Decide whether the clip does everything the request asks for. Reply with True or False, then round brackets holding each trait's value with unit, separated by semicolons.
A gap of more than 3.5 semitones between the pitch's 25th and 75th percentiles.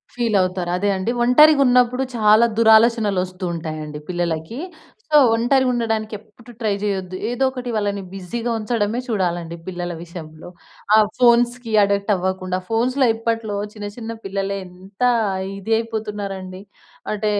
True (4.2 semitones)